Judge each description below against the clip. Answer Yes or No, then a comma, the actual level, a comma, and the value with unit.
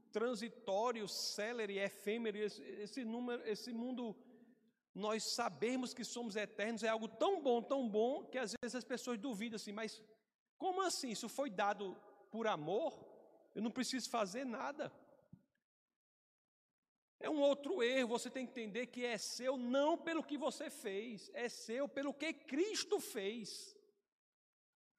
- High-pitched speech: Yes, high, 240 Hz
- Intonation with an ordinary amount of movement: Yes, average, 3.5 semitones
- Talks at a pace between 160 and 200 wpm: No, average, 145 wpm